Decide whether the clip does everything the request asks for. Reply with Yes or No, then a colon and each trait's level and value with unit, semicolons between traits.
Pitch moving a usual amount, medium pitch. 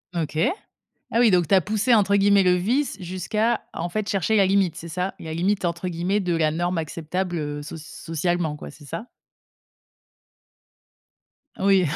Yes: average, 3.3 semitones; medium, 180 Hz